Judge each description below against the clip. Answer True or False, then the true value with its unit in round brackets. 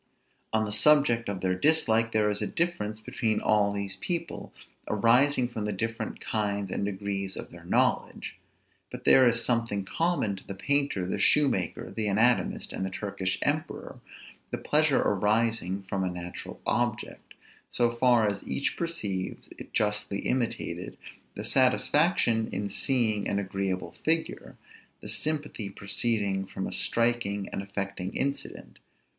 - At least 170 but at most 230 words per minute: False (150 wpm)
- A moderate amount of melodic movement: True (3.6 semitones)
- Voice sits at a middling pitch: False (110 Hz)